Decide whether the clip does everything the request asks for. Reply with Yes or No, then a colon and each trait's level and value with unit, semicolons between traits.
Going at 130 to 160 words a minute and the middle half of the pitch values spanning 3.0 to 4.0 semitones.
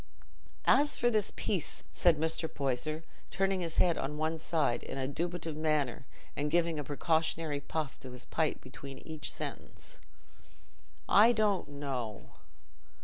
Yes: average, 145 wpm; average, 3.3 semitones